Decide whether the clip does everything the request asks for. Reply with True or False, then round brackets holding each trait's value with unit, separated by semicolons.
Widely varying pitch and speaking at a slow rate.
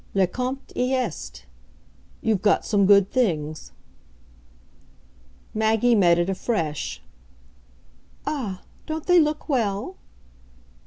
True (5.7 semitones; 100 wpm)